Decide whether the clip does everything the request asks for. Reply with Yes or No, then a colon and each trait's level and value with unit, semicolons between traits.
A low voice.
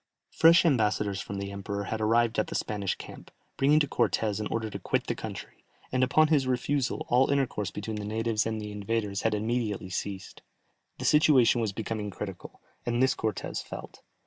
Yes: low, 110 Hz